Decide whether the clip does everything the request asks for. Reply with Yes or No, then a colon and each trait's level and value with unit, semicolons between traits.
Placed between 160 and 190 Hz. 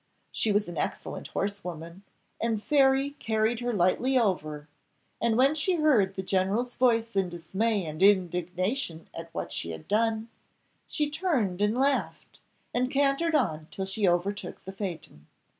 No: high, 205 Hz